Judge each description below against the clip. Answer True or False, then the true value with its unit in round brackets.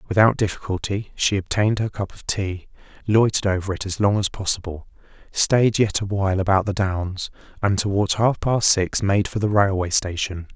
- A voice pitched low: True (100 Hz)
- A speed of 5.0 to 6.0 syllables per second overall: True (5.2 syllables/s)